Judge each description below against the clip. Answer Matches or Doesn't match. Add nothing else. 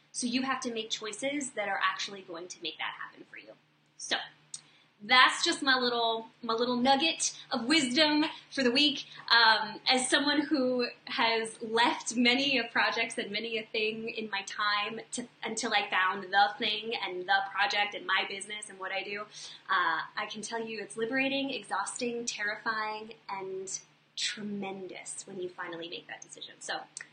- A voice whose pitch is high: Matches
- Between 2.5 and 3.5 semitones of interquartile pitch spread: Doesn't match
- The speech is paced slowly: Doesn't match